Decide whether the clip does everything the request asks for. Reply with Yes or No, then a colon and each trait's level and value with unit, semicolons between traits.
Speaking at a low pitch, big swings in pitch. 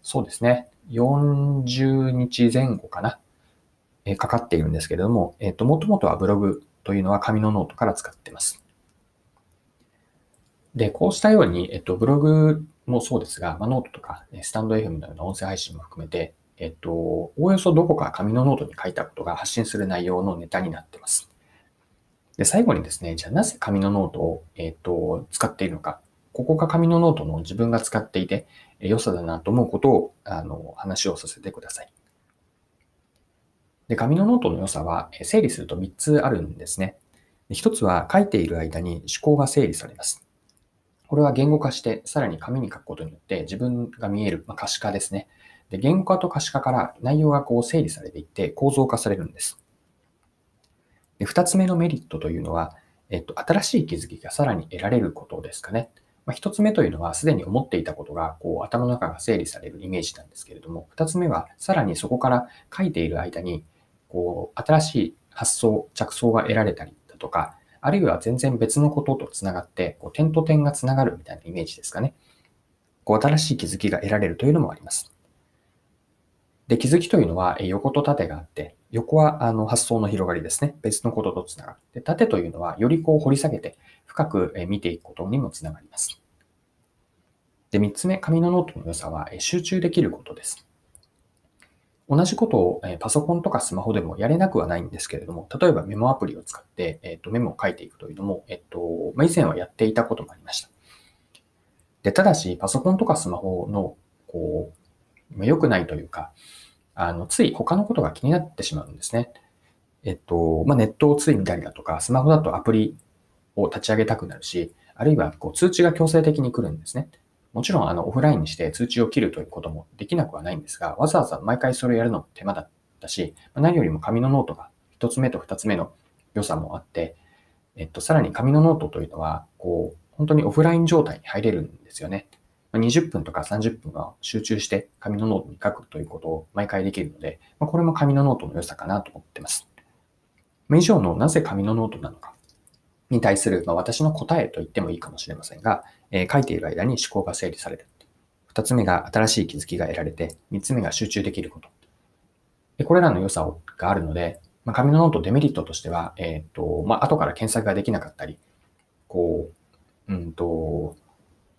Yes: low, 115 Hz; wide, 8.2 semitones